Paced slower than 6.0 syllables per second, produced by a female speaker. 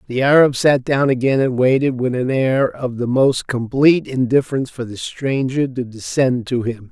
No: 4.9 syllables/s; male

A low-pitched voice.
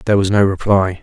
Yes: low, 100 Hz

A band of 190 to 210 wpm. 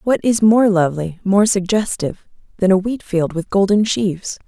No: average, 175 wpm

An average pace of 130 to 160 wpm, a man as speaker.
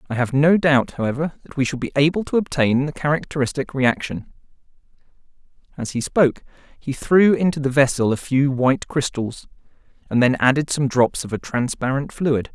No: average, 170 wpm; male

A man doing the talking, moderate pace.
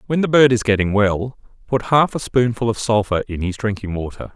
No: male; fast, 220 wpm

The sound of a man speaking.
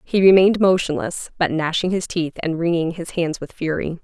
No: female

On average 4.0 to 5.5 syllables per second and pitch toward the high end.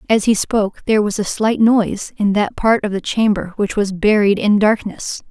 Yes: 5.0 syllables/s; high, 205 Hz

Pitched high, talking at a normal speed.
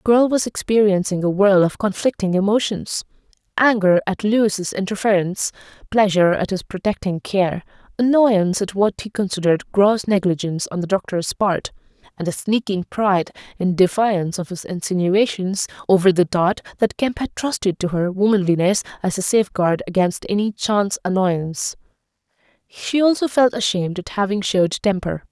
Yes: high, 195 Hz; average, 145 wpm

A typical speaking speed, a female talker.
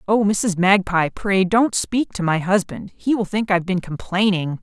Yes: average, 195 wpm; female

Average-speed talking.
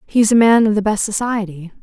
No: fast, 230 wpm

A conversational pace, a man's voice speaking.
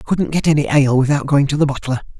No: fast, 275 wpm; male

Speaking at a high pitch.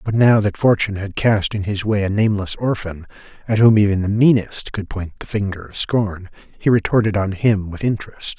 No: low, 105 Hz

